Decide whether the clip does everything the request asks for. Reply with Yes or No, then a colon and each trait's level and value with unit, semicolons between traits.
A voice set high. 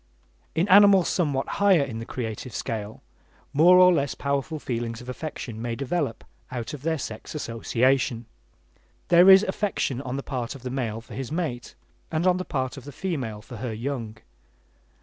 No: low, 135 Hz